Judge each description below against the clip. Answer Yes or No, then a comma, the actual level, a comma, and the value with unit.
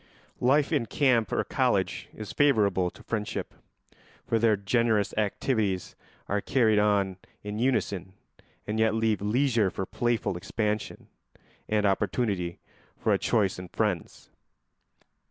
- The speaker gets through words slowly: Yes, slow, 125 wpm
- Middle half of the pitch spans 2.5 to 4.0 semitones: Yes, average, 2.8 semitones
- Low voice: Yes, low, 105 Hz